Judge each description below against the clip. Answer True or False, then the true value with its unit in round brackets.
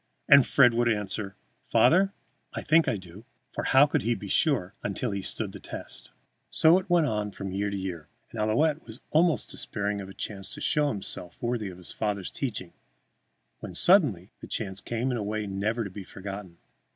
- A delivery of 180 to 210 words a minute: True (200 wpm)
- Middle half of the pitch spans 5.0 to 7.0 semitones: True (5.4 semitones)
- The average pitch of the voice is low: True (105 Hz)